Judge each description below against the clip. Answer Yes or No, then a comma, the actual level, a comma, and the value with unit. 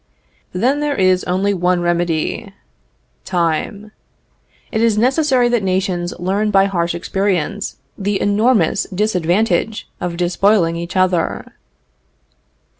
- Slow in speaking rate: Yes, slow, 110 wpm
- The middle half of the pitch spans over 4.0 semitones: No, average, 3.3 semitones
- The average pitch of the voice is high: Yes, high, 195 Hz